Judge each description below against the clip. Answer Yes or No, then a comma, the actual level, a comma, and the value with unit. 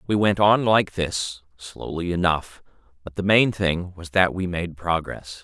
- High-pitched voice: No, very low, 90 Hz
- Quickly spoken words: No, average, 175 wpm